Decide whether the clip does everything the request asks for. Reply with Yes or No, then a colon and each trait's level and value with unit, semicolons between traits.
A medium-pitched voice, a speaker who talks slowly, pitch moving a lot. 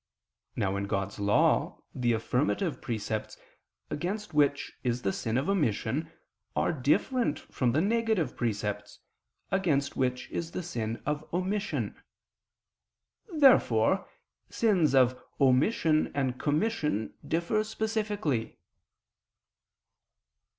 Yes: medium, 145 Hz; slow, 100 wpm; wide, 8.4 semitones